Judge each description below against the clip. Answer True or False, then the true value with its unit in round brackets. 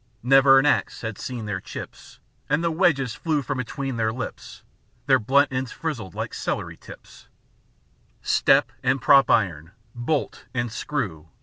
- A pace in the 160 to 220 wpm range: False (150 wpm)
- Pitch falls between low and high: False (130 Hz)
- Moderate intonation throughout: True (4.0 semitones)